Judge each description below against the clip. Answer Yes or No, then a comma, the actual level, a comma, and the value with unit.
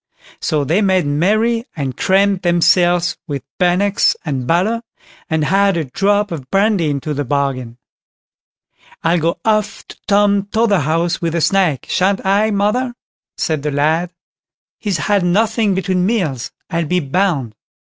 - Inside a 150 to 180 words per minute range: No, average, 140 wpm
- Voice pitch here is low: No, medium, 180 Hz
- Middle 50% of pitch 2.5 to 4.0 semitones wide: No, average, 4.7 semitones